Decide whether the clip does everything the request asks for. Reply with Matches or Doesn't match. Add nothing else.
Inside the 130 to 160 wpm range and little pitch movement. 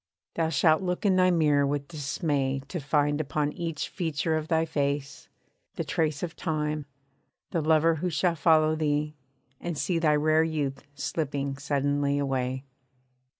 Matches